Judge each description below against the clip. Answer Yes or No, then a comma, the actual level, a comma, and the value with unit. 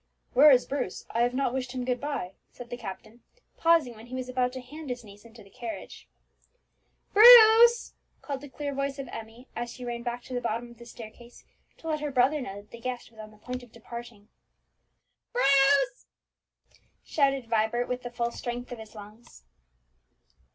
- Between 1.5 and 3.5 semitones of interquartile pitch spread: Yes, average, 2.8 semitones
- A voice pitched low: No, high, 245 Hz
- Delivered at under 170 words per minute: No, average, 195 wpm